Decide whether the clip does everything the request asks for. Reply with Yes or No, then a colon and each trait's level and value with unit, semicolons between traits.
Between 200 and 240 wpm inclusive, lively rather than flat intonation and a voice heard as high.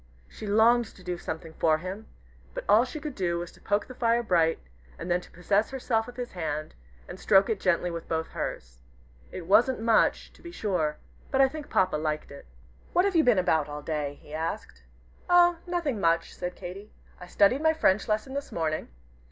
Yes: fast, 205 wpm; wide, 6.7 semitones; high, 195 Hz